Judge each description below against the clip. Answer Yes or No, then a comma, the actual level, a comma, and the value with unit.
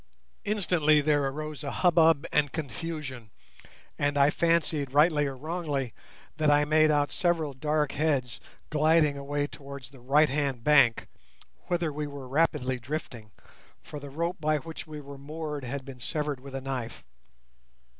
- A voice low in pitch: No, medium, 145 Hz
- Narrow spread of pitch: Yes, narrow, 2.3 semitones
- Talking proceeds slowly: No, average, 155 wpm